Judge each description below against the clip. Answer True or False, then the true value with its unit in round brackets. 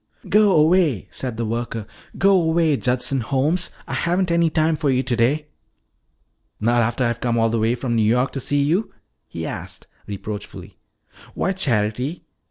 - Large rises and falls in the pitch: True (5.7 semitones)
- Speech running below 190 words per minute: True (165 wpm)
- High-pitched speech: False (130 Hz)